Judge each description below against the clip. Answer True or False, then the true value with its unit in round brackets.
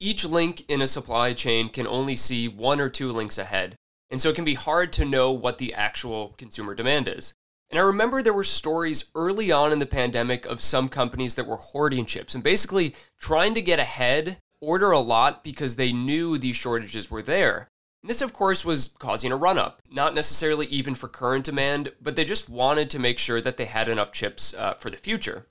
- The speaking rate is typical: False (220 wpm)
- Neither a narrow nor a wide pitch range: True (4.4 semitones)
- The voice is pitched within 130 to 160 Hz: True (135 Hz)